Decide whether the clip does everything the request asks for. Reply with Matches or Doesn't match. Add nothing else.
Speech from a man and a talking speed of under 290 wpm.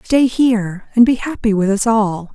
Doesn't match